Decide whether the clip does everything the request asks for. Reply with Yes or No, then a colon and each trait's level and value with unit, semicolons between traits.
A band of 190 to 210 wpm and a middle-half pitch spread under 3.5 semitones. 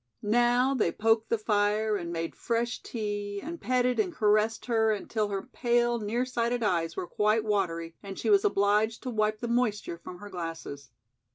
No: average, 180 wpm; average, 2.8 semitones